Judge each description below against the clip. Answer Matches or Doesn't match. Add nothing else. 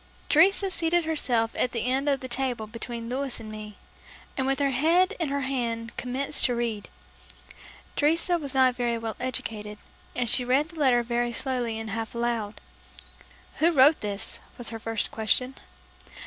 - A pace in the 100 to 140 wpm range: Doesn't match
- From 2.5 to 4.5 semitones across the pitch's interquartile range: Matches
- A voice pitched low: Doesn't match